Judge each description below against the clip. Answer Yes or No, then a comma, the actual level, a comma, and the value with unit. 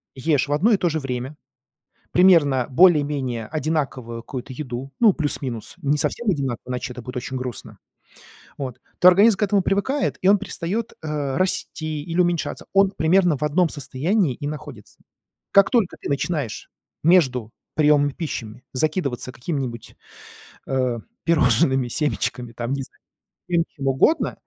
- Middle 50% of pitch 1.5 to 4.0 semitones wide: No, average, 5.3 semitones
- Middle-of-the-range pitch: Yes, medium, 145 Hz